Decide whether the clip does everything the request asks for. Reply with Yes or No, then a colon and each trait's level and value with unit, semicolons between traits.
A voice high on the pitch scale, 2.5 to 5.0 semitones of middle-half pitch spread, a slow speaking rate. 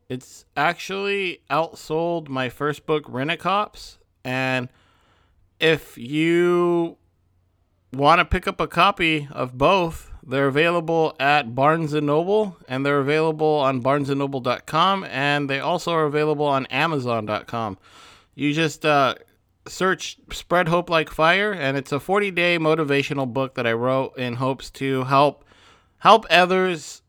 No: medium, 145 Hz; average, 4.3 semitones; slow, 130 wpm